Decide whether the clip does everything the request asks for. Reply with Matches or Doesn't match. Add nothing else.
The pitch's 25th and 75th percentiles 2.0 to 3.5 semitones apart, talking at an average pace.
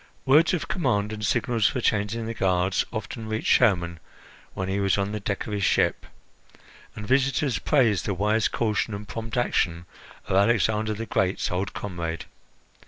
Matches